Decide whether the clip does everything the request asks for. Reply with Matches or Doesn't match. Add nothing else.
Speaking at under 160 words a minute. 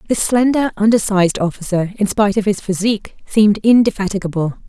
Matches